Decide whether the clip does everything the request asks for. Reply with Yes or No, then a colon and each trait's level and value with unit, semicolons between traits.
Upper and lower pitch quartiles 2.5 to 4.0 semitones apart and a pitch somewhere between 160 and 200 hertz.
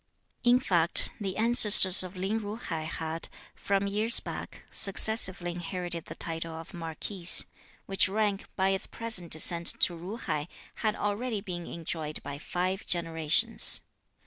Yes: average, 3.7 semitones; medium, 185 Hz